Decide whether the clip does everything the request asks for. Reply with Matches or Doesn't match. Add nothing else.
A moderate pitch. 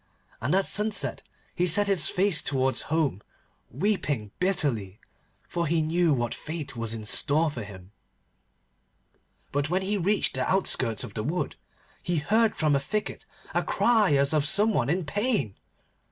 Matches